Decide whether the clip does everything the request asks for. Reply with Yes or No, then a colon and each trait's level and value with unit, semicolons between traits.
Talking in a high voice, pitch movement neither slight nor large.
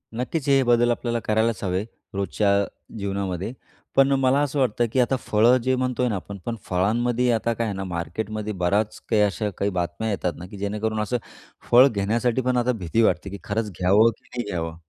No: low, 110 Hz; average, 3.5 semitones